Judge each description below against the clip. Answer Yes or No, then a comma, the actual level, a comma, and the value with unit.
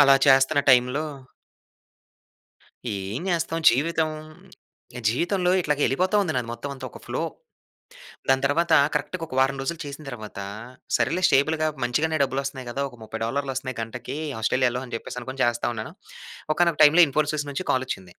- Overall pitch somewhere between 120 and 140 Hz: Yes, low, 135 Hz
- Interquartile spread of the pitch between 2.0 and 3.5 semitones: No, average, 4.2 semitones